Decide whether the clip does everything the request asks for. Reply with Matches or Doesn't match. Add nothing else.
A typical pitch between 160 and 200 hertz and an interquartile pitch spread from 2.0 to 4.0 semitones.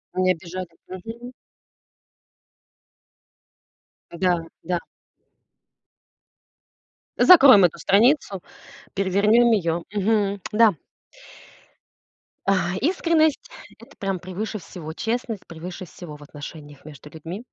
Doesn't match